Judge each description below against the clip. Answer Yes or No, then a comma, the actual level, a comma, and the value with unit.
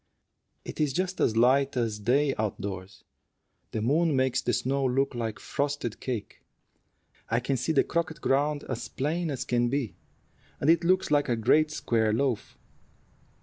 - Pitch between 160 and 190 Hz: No, low, 130 Hz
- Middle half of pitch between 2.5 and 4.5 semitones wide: Yes, average, 4.1 semitones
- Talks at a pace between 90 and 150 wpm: No, average, 160 wpm